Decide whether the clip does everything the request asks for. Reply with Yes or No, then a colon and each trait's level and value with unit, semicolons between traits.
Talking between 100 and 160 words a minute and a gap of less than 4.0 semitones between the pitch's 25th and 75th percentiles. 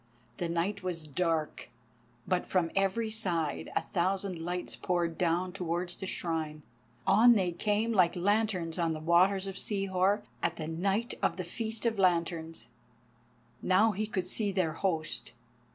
Yes: average, 150 wpm; average, 2.9 semitones